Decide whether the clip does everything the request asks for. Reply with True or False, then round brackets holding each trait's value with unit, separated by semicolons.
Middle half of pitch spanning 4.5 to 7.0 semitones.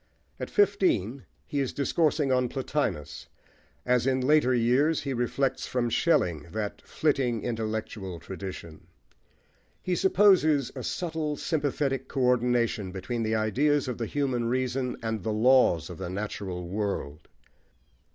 True (5.1 semitones)